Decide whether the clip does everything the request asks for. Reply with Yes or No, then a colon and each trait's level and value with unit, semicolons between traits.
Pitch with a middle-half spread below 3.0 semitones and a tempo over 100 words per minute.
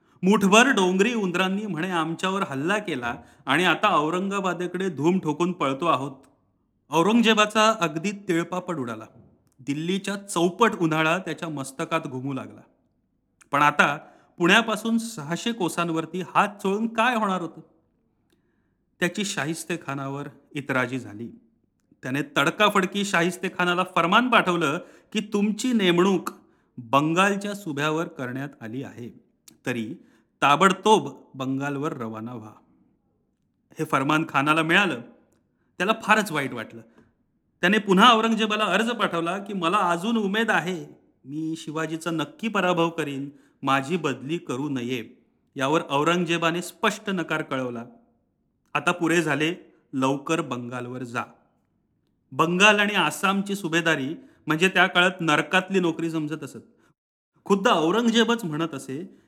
No: wide, 5.4 semitones; average, 110 wpm